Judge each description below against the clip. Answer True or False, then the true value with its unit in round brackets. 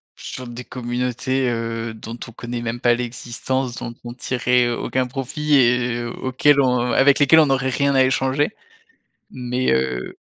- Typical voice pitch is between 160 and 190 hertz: False (125 Hz)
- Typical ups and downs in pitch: False (1.7 semitones)